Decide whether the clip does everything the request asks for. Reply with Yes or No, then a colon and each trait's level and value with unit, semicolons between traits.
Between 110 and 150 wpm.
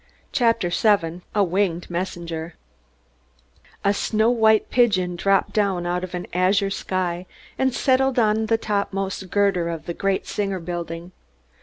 Yes: average, 145 wpm